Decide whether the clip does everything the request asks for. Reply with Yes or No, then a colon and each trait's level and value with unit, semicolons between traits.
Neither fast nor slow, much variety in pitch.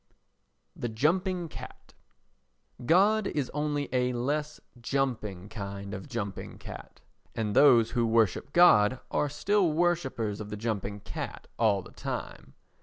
No: slow, 130 wpm; wide, 6.2 semitones